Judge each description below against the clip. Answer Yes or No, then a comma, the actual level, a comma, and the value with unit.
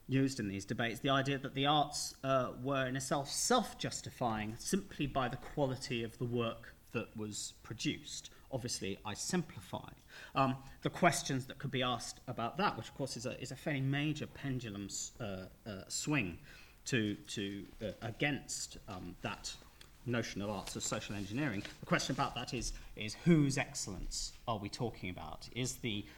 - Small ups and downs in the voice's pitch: No, average, 4.5 semitones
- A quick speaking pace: No, average, 175 wpm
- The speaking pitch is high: No, low, 125 Hz